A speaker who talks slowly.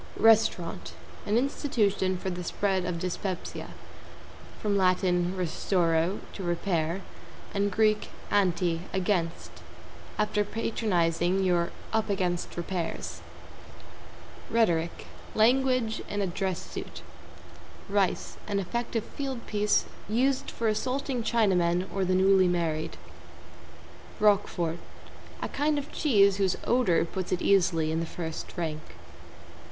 Yes: slow, 115 wpm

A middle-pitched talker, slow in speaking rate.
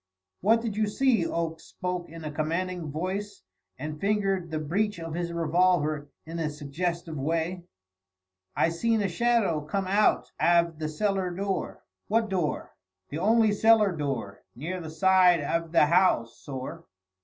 No: medium, 175 Hz; average, 155 wpm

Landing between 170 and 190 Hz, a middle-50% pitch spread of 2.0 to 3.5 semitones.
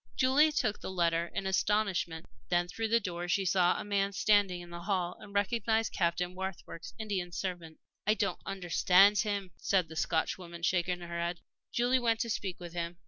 Yes: medium, 185 Hz; average, 2.9 semitones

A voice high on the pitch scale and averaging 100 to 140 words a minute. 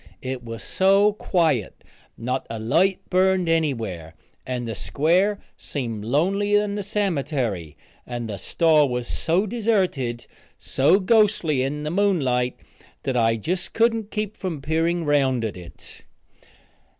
No: medium, 150 Hz; slow, 135 wpm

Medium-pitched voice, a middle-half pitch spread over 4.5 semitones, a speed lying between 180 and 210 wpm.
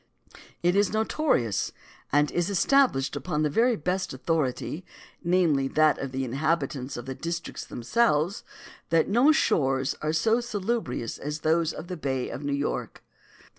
No: medium, 155 Hz; wide, 5.6 semitones; average, 150 wpm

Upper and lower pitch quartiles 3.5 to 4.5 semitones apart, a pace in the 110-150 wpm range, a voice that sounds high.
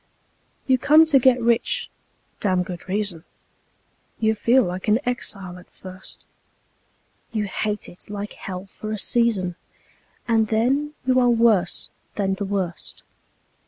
Yes: average, 4.0 semitones; slow, 135 wpm; high, 210 Hz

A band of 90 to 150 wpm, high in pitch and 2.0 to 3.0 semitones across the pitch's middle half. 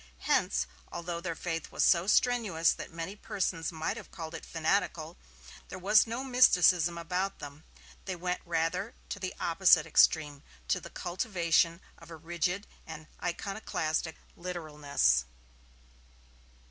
No: slow, 135 wpm; medium, 170 Hz; narrow, 2.5 semitones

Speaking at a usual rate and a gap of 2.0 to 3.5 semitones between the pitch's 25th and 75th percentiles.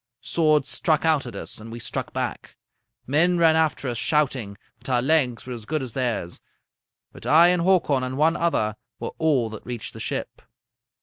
No: average, 190 wpm; average, 5.0 semitones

